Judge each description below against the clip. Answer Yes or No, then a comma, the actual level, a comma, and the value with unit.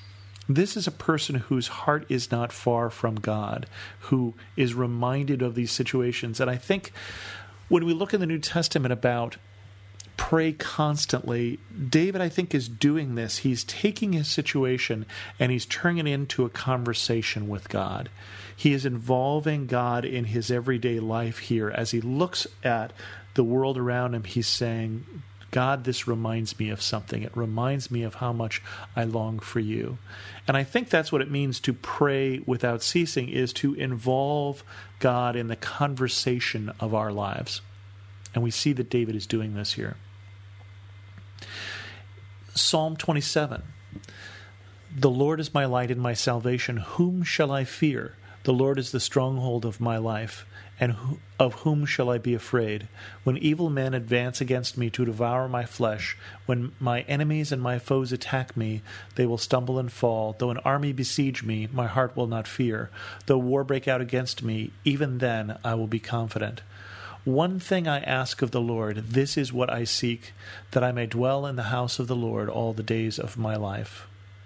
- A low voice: Yes, low, 120 Hz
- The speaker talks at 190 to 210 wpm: No, average, 175 wpm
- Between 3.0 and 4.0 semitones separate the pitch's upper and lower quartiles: Yes, average, 3.7 semitones